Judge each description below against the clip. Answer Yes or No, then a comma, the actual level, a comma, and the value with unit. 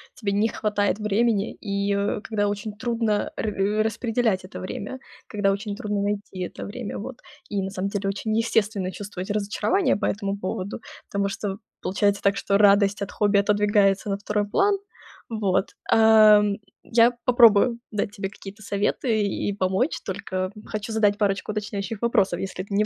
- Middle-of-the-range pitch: No, high, 205 Hz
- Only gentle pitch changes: Yes, narrow, 1.5 semitones